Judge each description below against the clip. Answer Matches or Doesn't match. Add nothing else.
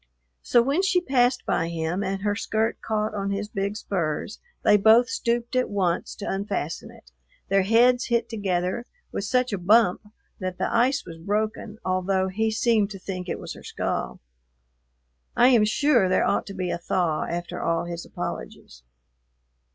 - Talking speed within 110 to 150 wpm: Doesn't match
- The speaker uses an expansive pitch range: Doesn't match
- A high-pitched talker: Matches